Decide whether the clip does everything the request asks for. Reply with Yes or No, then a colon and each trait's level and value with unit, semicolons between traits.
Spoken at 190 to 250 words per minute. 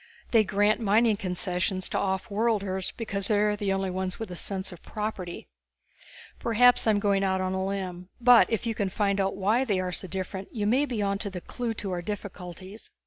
Yes: average, 200 wpm